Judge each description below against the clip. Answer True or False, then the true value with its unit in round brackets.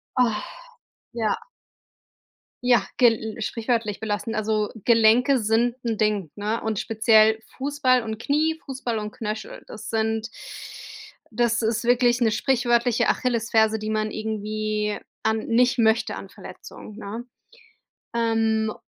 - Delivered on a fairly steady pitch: True (1.8 semitones)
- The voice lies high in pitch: True (225 Hz)